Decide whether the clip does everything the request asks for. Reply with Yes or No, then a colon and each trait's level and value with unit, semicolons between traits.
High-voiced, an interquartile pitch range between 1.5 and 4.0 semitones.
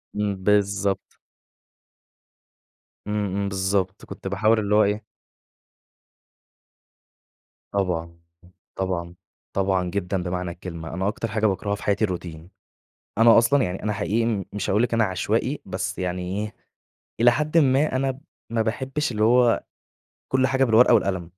No: low, 100 Hz; average, 3.6 semitones